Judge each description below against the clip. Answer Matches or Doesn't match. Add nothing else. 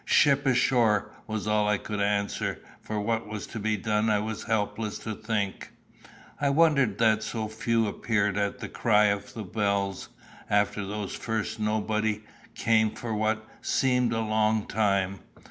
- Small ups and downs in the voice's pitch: Matches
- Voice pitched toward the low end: Matches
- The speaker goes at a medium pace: Matches